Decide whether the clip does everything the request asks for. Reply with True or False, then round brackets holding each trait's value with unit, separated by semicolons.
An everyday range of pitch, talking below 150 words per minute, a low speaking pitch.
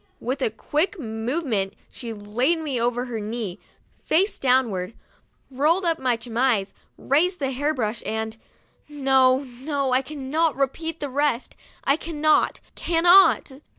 False (4.7 semitones; 140 wpm; 265 Hz)